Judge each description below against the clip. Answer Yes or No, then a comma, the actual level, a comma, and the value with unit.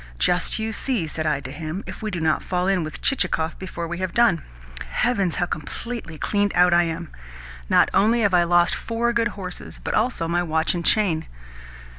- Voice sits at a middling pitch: Yes, medium, 180 Hz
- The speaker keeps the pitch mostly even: No, average, 4.6 semitones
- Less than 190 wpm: No, average, 200 wpm